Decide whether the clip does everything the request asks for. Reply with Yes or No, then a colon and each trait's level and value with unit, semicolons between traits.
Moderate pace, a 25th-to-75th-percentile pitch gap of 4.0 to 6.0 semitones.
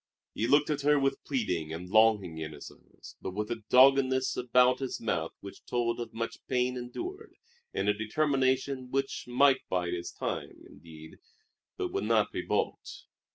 Yes: average, 170 wpm; average, 5.2 semitones